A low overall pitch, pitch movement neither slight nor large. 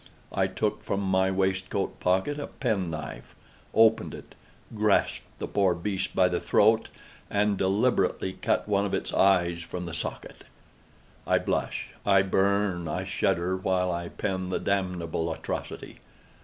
No: very low, 95 Hz; narrow, 2.0 semitones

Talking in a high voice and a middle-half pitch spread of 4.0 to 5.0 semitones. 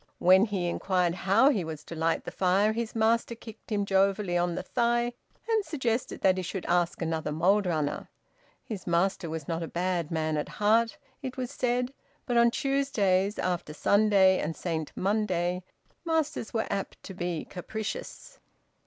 Yes: high, 195 Hz; average, 4.7 semitones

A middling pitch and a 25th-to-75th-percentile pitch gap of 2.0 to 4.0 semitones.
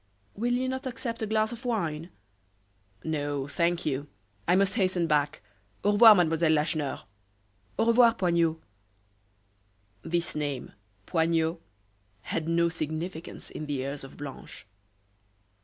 No: medium, 165 Hz; average, 5.2 semitones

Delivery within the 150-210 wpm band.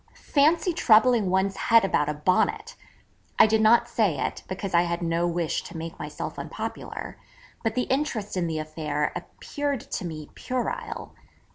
Yes: average, 160 wpm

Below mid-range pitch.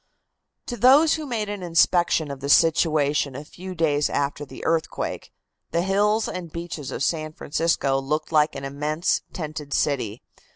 No: medium, 155 Hz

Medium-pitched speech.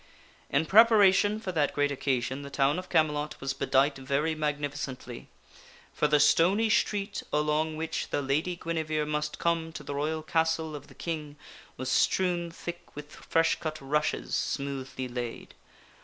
Yes: medium, 150 Hz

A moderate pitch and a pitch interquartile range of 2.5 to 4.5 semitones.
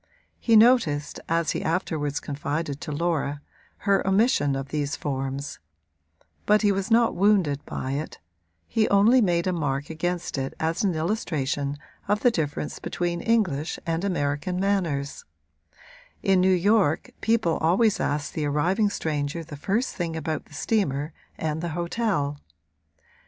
No: medium, 165 Hz; wide, 5.4 semitones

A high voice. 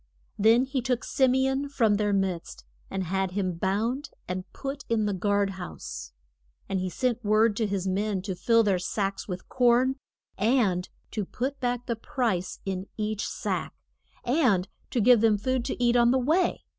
Yes: high, 215 Hz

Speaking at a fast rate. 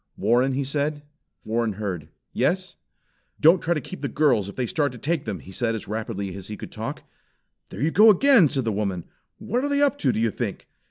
Yes: fast, 225 wpm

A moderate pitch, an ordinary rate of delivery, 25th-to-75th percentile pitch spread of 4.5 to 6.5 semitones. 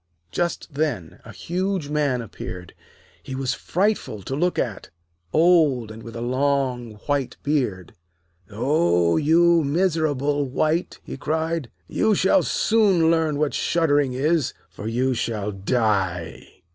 No: medium, 145 Hz; slow, 130 wpm; wide, 5.6 semitones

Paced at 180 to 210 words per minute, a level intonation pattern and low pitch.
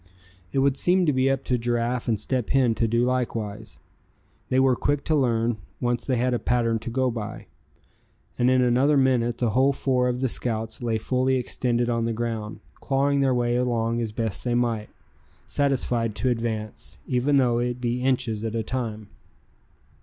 Yes: average, 185 wpm; narrow, 2.1 semitones; low, 120 Hz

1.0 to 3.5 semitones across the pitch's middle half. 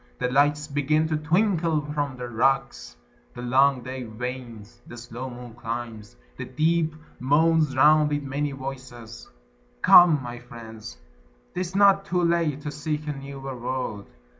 No: average, 4.0 semitones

